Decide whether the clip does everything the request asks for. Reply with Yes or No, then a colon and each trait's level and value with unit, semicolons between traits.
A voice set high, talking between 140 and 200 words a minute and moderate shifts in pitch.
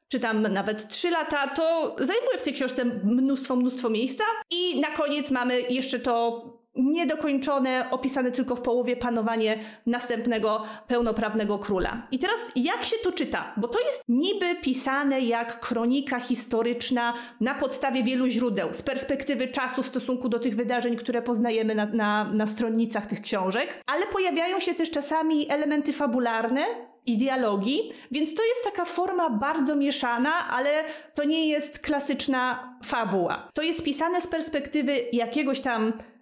Yes: very high, 255 Hz; average, 150 wpm; average, 4.0 semitones